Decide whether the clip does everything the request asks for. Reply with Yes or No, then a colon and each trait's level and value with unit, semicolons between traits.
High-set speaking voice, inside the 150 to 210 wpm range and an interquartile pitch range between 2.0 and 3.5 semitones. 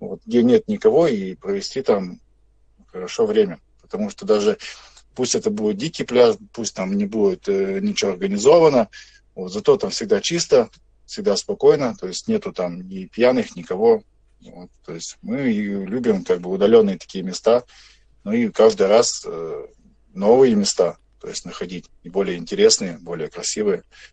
Yes: high, 215 Hz; average, 155 wpm; average, 2.9 semitones